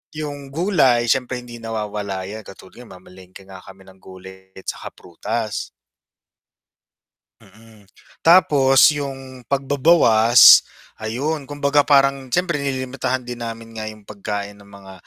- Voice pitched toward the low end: Yes, low, 120 Hz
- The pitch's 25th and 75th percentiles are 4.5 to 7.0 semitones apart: Yes, average, 5.3 semitones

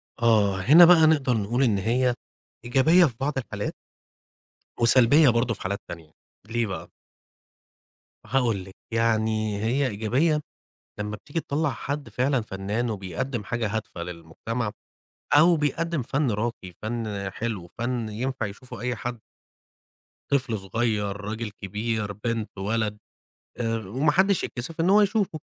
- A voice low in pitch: Yes, low, 115 Hz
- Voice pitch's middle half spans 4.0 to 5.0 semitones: Yes, average, 4.3 semitones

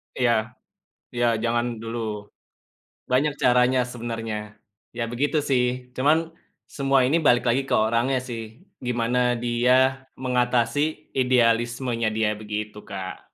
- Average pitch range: No, narrow, 1.9 semitones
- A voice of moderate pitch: No, low, 120 Hz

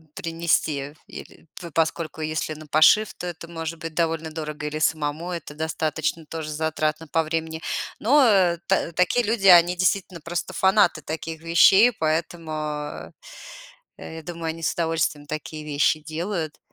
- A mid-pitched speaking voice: Yes, medium, 160 Hz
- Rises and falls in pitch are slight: Yes, narrow, 1.8 semitones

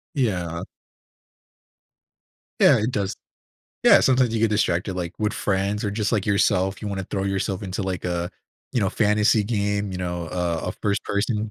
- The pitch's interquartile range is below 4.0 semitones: Yes, narrow, 2.5 semitones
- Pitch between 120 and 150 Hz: No, low, 100 Hz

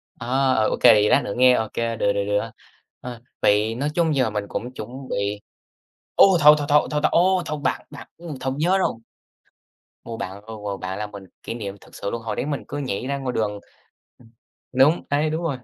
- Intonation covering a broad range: Yes, wide, 5.7 semitones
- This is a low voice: Yes, low, 125 Hz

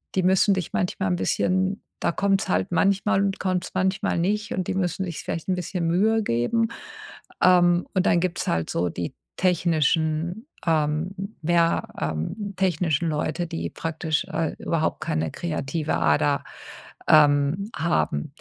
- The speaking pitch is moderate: Yes, medium, 170 Hz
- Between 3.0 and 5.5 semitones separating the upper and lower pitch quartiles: Yes, average, 3.7 semitones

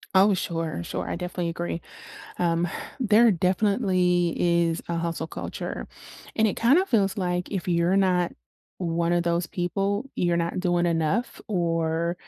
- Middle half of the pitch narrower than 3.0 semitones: Yes, narrow, 2.4 semitones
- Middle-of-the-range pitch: Yes, medium, 175 Hz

